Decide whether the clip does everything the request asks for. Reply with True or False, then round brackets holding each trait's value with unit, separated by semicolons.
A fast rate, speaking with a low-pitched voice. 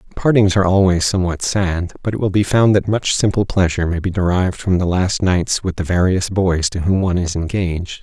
True (225 wpm; 95 Hz)